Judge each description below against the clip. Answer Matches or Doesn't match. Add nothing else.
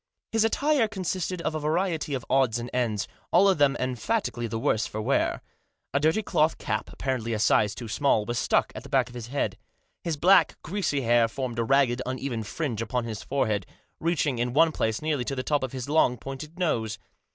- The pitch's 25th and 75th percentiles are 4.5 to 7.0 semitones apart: Matches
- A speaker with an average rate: Doesn't match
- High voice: Doesn't match